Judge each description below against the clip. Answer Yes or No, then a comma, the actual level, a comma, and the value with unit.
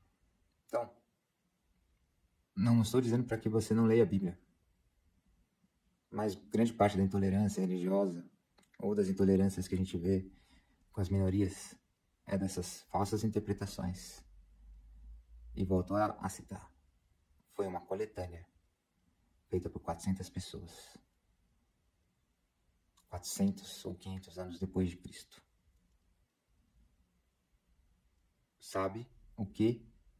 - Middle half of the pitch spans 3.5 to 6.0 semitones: No, average, 2.9 semitones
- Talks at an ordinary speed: No, slow, 105 wpm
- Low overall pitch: Yes, very low, 95 Hz